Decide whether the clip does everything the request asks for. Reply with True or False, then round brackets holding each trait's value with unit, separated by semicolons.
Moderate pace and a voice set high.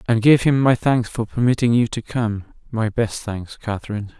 False (185 wpm; 115 Hz)